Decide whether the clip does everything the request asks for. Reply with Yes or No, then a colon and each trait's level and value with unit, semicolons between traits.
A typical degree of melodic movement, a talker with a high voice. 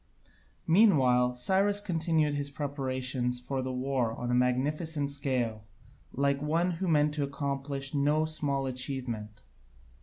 No: average, 3.1 semitones; medium, 140 Hz